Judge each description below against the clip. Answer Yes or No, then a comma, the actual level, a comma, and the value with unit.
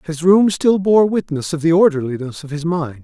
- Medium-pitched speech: Yes, medium, 165 Hz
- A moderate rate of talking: No, fast, 215 wpm